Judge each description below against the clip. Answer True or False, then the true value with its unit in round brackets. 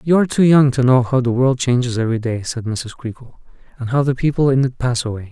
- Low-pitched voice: True (125 Hz)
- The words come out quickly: True (260 wpm)